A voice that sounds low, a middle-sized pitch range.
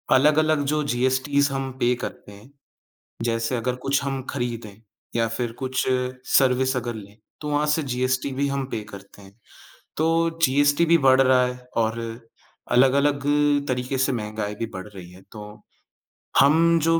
Yes: low, 130 Hz; average, 3.6 semitones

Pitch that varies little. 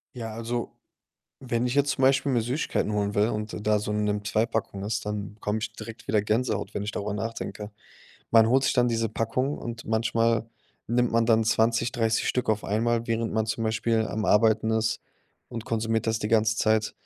Yes: narrow, 1.4 semitones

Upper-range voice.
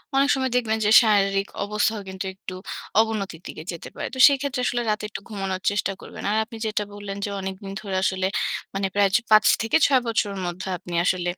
Yes: high, 205 Hz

